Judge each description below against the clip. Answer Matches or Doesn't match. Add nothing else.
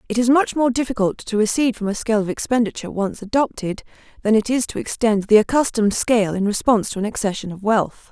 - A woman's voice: Matches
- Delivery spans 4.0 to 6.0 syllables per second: Doesn't match